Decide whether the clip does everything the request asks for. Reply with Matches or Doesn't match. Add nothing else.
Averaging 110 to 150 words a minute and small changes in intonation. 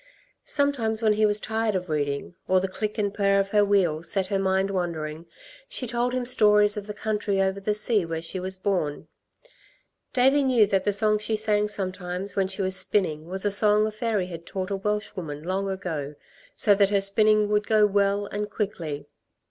Doesn't match